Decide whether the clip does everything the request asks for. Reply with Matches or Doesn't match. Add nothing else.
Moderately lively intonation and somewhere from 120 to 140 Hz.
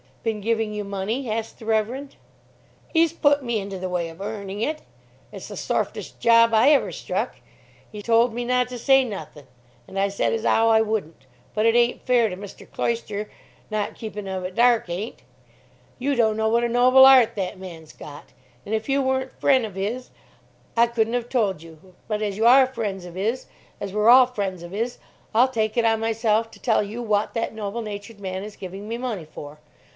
Doesn't match